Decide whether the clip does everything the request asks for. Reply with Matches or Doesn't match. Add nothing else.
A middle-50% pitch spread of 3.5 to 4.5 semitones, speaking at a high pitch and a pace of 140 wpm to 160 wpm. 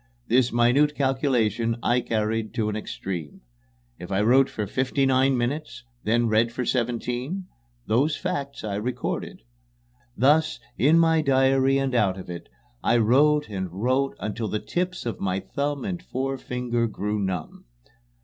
Doesn't match